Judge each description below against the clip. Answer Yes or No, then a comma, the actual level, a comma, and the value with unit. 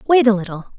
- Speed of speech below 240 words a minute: Yes, fast, 230 wpm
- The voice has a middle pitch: No, high, 225 Hz